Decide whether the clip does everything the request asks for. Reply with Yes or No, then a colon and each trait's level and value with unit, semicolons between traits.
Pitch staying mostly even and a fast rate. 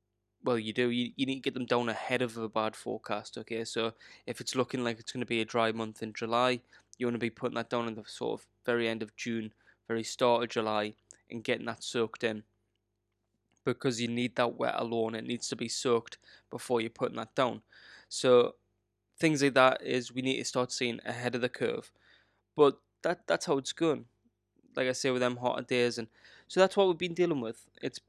Yes: narrow, 1.9 semitones; fast, 220 wpm